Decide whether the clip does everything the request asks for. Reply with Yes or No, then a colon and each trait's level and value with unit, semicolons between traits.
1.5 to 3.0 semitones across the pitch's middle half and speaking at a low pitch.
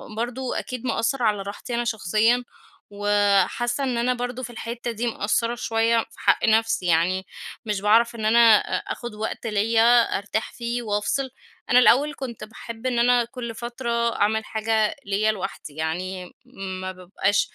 No: average, 2.7 semitones; high, 225 Hz